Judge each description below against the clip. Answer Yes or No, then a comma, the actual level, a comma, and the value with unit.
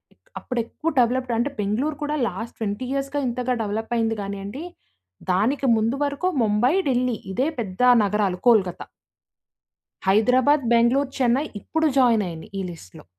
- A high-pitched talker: Yes, high, 235 Hz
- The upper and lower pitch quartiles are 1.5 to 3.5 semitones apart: No, average, 4.2 semitones